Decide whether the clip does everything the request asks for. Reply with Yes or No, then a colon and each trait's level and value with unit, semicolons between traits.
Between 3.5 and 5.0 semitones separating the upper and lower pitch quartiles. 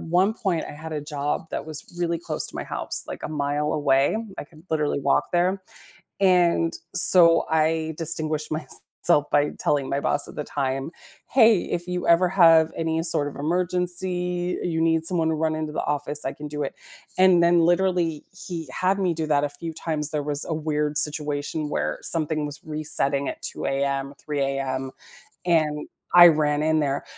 No: average, 2.7 semitones